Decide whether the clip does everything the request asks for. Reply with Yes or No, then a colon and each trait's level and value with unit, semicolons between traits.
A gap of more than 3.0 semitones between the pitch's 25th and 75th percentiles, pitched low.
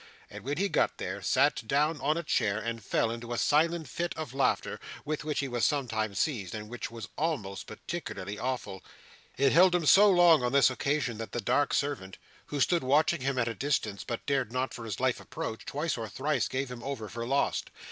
Yes: average, 4.6 semitones; low, 130 Hz